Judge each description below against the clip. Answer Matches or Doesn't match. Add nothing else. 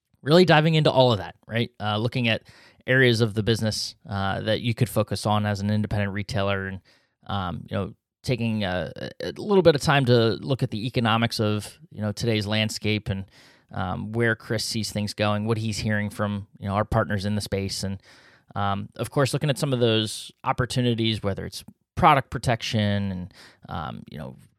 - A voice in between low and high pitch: Doesn't match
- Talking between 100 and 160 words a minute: Doesn't match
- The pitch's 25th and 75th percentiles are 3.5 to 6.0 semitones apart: Doesn't match